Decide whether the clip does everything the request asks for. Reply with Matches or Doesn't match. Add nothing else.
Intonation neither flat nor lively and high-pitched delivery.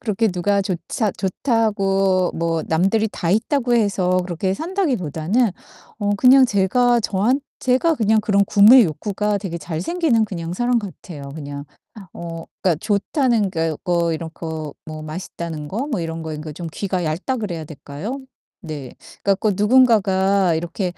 Matches